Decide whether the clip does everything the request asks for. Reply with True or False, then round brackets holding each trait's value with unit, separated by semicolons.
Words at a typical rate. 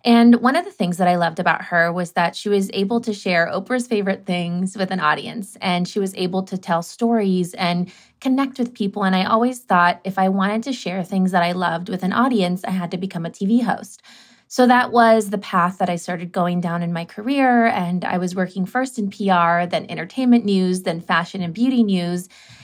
False (225 wpm)